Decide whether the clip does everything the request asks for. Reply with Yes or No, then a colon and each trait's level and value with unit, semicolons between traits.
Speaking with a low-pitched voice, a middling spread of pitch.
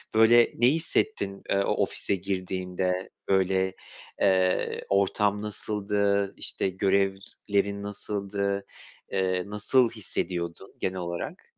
No: low, 100 Hz; narrow, 1.6 semitones